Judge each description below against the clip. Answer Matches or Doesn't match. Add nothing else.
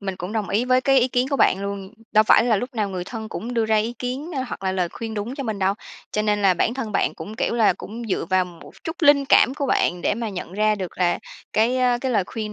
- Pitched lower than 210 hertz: Doesn't match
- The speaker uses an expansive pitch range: Doesn't match